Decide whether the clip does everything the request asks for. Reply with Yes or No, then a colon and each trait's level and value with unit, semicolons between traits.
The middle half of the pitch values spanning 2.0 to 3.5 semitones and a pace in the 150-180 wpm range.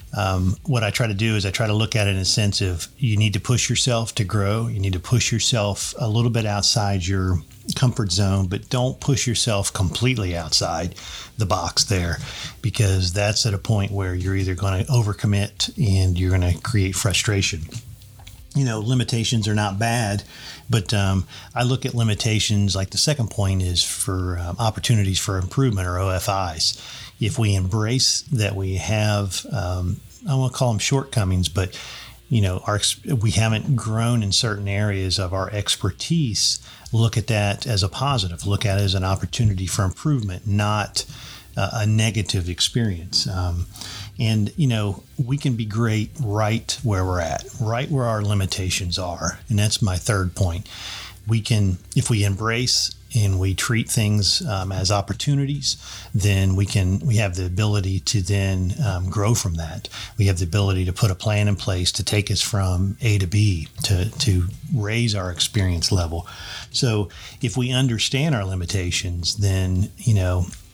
Yes: average, 3.2 semitones; average, 175 wpm